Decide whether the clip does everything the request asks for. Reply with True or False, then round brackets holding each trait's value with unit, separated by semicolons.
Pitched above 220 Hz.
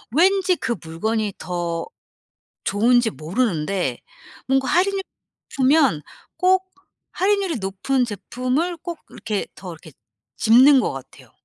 True (245 Hz)